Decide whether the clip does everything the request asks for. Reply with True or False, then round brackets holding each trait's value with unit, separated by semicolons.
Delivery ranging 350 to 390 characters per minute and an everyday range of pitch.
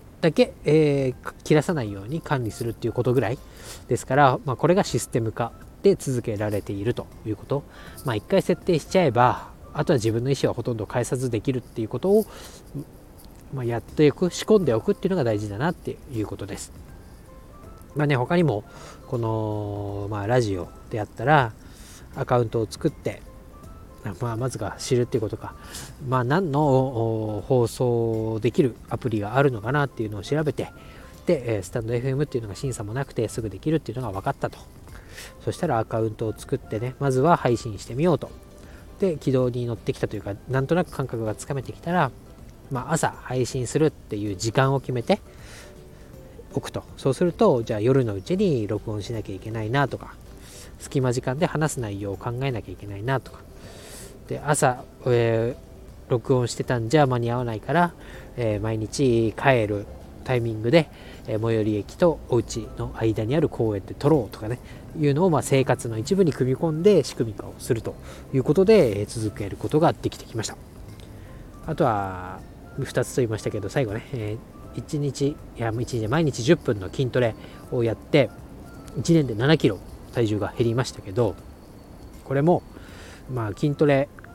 True (360 characters per minute; 4.7 semitones)